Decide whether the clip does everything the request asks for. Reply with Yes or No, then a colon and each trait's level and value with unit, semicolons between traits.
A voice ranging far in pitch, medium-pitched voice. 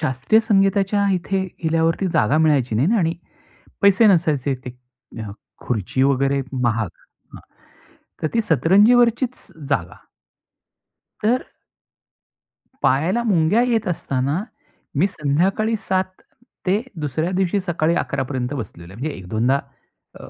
Yes: wide, 6.8 semitones; medium, 160 Hz